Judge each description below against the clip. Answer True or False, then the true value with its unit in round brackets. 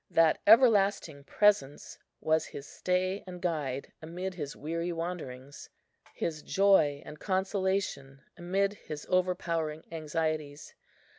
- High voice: False (165 Hz)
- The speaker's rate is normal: False (105 wpm)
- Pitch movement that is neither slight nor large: True (3.9 semitones)